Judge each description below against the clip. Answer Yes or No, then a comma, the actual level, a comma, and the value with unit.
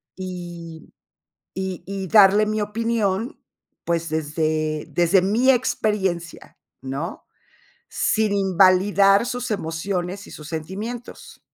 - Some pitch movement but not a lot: Yes, average, 3.8 semitones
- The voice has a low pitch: No, high, 190 Hz